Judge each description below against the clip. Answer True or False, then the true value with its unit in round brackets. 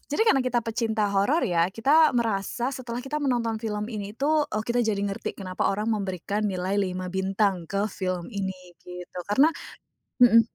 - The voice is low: False (210 Hz)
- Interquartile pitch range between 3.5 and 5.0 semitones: True (4.0 semitones)